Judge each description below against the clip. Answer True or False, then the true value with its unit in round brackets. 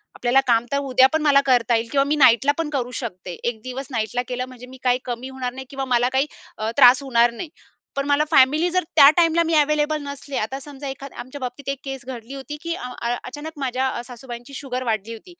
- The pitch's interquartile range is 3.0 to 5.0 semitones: False (2.6 semitones)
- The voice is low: False (260 Hz)